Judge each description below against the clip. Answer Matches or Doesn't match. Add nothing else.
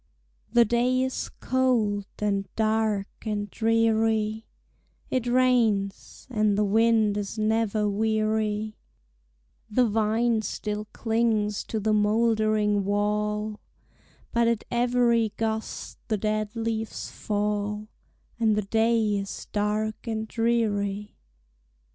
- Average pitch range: Doesn't match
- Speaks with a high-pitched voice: Matches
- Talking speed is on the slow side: Matches